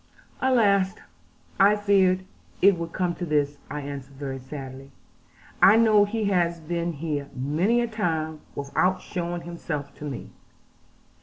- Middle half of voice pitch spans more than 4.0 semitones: Yes, wide, 5.4 semitones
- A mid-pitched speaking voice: Yes, medium, 170 Hz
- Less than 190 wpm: Yes, average, 140 wpm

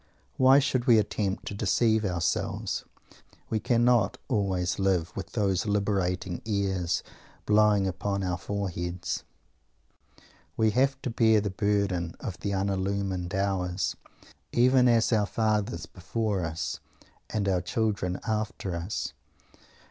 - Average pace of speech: No, slow, 120 wpm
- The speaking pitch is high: No, low, 100 Hz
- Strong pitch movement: No, average, 3.1 semitones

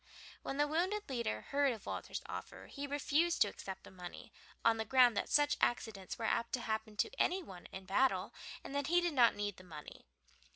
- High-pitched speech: Yes, high, 240 Hz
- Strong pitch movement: Yes, wide, 6.1 semitones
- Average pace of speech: No, fast, 210 wpm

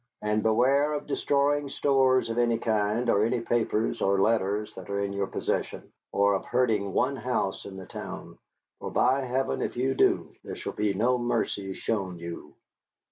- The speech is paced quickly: No, average, 180 wpm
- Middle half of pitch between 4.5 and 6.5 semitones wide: No, average, 4.1 semitones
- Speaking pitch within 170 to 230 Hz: No, low, 115 Hz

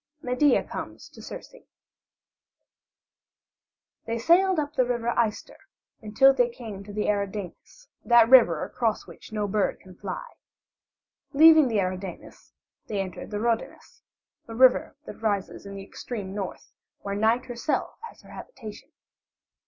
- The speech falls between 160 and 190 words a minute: No, slow, 135 wpm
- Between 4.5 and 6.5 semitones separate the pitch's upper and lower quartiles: No, average, 3.8 semitones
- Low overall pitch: No, high, 225 Hz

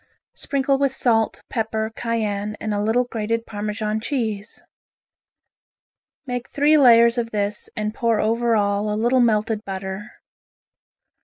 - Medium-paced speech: No, slow, 130 wpm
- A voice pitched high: Yes, high, 225 Hz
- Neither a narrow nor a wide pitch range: No, narrow, 2.2 semitones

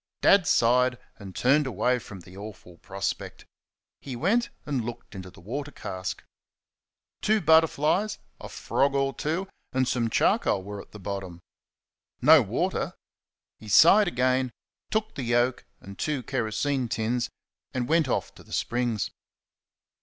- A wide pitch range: Yes, wide, 5.7 semitones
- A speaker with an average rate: Yes, average, 145 wpm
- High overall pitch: No, low, 125 Hz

